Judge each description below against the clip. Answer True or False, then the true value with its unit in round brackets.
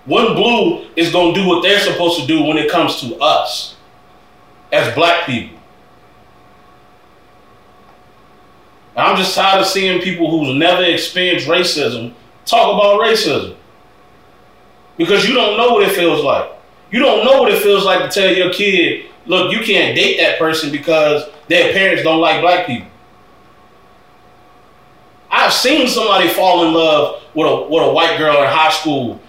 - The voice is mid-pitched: True (180 Hz)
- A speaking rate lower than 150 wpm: False (165 wpm)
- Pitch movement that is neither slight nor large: True (3.7 semitones)